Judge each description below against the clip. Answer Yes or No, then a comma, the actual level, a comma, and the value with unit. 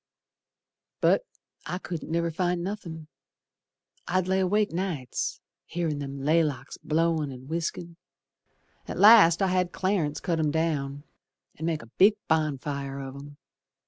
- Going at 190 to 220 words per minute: No, slow, 135 wpm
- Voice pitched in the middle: Yes, medium, 165 Hz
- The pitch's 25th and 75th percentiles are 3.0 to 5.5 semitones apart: Yes, average, 3.7 semitones